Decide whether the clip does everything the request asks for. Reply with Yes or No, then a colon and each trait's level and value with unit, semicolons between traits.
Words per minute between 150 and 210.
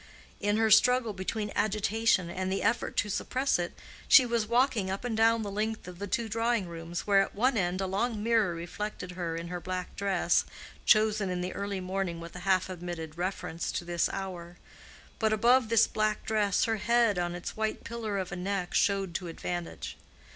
Yes: average, 200 wpm